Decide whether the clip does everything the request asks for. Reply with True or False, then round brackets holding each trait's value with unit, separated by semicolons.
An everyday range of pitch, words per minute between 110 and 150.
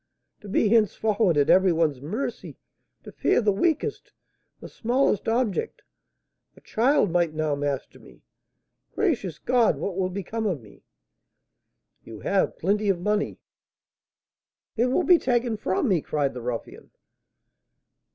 False (6.2 semitones; 135 wpm)